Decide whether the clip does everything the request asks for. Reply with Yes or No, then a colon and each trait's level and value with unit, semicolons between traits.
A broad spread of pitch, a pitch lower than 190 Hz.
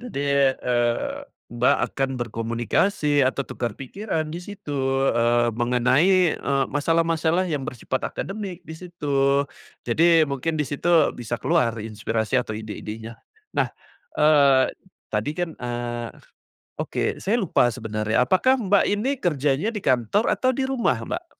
Yes: wide, 6.7 semitones; medium, 140 Hz